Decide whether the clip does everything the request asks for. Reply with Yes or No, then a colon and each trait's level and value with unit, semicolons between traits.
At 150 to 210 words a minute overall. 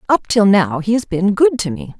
No: fast, 270 wpm